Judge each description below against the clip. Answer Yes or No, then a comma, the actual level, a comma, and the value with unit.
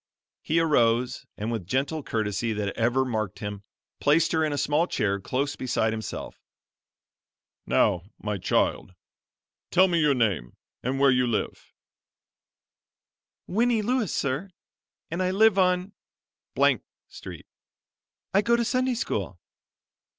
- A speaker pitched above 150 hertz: No, low, 135 Hz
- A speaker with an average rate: No, slow, 130 wpm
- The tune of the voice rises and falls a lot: Yes, wide, 8.6 semitones